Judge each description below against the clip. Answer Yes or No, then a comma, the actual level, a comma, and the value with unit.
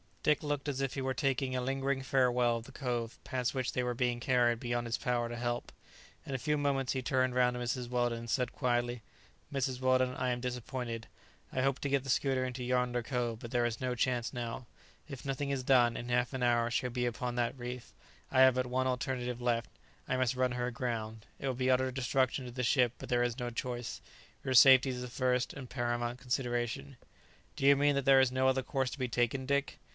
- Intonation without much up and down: Yes, narrow, 1.5 semitones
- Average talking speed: No, fast, 230 wpm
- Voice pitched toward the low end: Yes, low, 125 Hz